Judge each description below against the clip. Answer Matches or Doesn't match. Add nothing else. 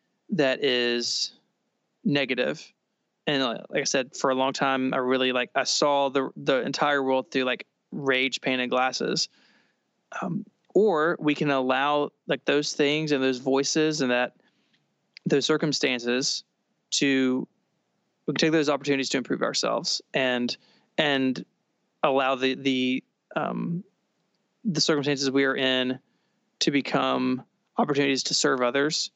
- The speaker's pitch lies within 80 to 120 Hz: Doesn't match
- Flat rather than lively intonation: Matches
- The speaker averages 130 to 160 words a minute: Matches